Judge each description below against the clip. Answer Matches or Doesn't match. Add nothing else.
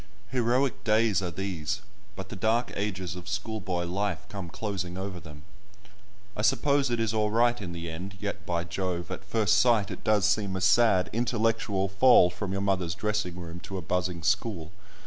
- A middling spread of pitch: Matches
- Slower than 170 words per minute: Doesn't match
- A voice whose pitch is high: Doesn't match